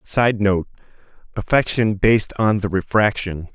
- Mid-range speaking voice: No, low, 105 Hz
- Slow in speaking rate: Yes, slow, 100 wpm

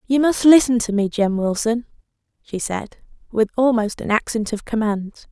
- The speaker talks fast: No, average, 170 wpm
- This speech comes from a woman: Yes, female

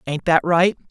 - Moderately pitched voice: Yes, medium, 170 Hz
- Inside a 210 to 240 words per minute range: No, average, 200 wpm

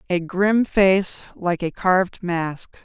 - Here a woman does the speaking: Yes, female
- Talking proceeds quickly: No, average, 150 wpm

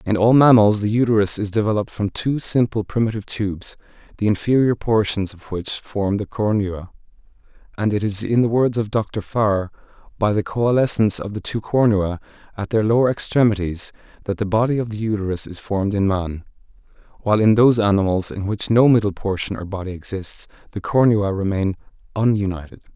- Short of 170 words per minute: No, average, 175 wpm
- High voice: No, low, 105 Hz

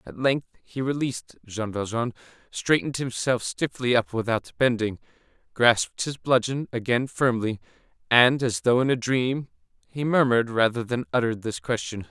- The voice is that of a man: Yes, male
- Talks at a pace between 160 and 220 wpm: No, average, 150 wpm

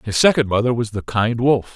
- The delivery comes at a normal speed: No, fast, 240 wpm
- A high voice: No, low, 115 Hz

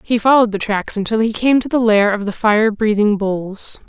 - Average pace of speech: No, fast, 230 wpm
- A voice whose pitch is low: No, high, 215 Hz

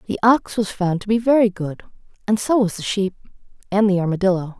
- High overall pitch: Yes, high, 200 Hz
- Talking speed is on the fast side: Yes, fast, 210 wpm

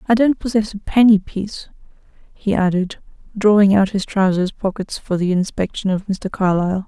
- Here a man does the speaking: No, female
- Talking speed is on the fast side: No, average, 165 wpm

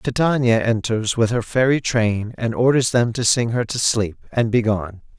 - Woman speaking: No, male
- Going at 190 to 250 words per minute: Yes, average, 195 wpm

